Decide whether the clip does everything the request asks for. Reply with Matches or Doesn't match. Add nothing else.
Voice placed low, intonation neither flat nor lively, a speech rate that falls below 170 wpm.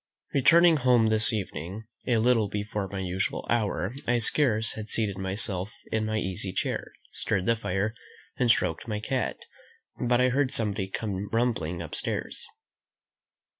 Matches